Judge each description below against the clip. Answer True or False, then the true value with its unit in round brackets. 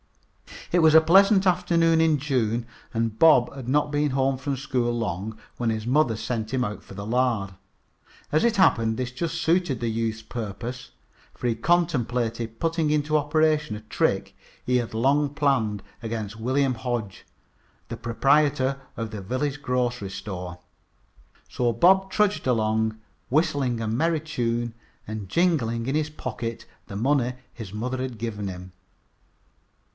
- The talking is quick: False (150 wpm)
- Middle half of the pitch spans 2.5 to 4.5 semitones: False (4.9 semitones)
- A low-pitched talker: True (125 Hz)